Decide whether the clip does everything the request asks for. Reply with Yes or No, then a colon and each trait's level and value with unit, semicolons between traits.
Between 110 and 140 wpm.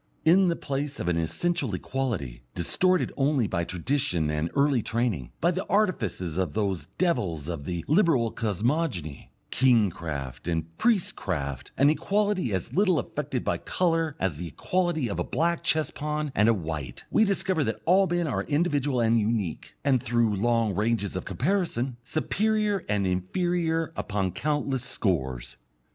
No: average, 155 wpm